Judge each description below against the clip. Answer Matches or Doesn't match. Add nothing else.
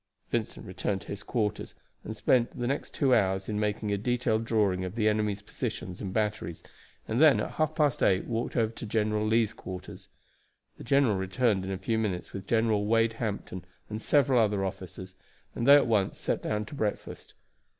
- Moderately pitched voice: Doesn't match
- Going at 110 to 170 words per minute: Doesn't match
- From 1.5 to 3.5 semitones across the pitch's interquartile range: Matches